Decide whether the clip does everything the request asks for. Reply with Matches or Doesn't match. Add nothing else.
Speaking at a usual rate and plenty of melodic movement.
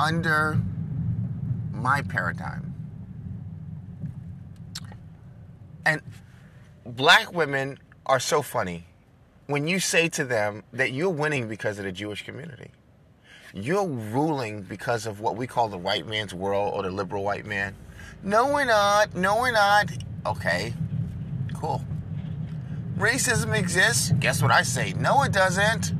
Doesn't match